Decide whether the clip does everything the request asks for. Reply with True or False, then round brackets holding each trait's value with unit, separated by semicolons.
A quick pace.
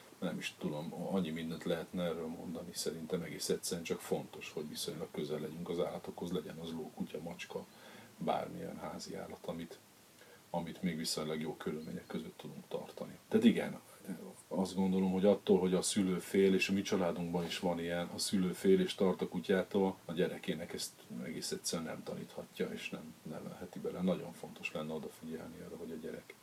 True (175 wpm)